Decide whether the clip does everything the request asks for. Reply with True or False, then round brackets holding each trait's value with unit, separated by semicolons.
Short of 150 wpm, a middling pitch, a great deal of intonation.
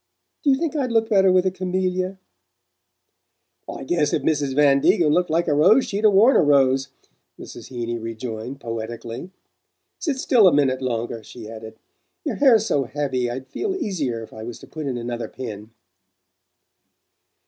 False (170 wpm; 145 Hz; 7.7 semitones)